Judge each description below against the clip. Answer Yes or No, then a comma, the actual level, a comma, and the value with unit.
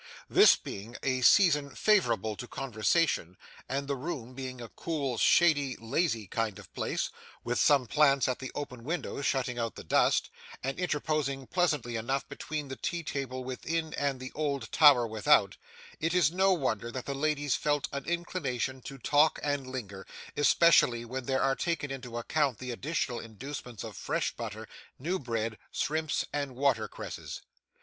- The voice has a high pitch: No, low, 135 Hz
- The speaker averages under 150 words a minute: No, average, 160 wpm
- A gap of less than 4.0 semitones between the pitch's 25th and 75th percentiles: Yes, average, 3.6 semitones